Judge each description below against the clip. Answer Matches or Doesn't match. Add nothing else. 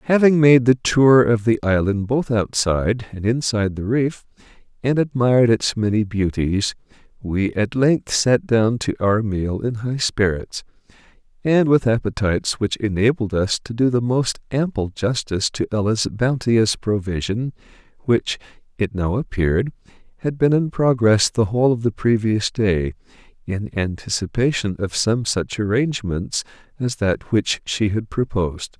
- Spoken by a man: Matches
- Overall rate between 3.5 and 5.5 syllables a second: Matches